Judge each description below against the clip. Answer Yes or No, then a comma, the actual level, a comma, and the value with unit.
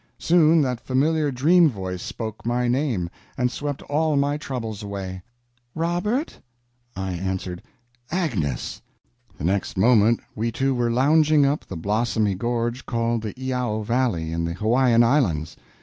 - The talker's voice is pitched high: No, low, 120 Hz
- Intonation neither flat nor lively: No, wide, 5.9 semitones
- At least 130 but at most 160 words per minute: Yes, average, 140 wpm